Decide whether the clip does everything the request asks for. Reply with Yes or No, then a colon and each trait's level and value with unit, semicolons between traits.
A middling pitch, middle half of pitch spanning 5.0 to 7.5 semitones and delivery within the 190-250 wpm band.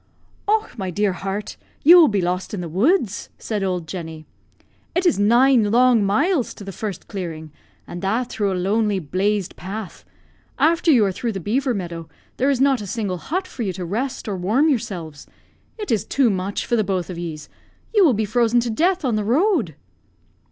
No: high, 210 Hz; wide, 5.5 semitones; average, 200 wpm